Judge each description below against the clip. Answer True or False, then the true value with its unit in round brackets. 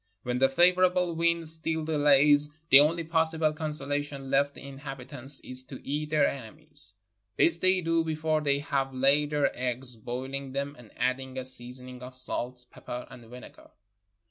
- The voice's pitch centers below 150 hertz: True (140 Hz)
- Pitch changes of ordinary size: True (3.2 semitones)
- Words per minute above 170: False (160 wpm)